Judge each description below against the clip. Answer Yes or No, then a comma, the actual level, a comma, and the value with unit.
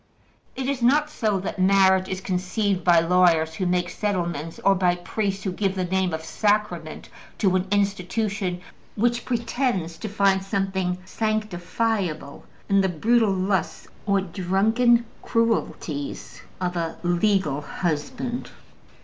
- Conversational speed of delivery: No, slow, 130 wpm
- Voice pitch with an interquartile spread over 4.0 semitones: No, average, 3.3 semitones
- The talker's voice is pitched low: No, high, 190 Hz